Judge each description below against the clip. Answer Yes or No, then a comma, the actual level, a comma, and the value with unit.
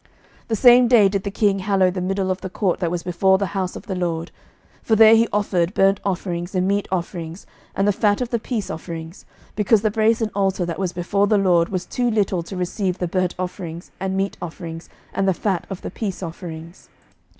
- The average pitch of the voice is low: No, high, 190 Hz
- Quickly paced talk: Yes, fast, 220 wpm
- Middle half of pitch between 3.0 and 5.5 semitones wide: No, narrow, 2.5 semitones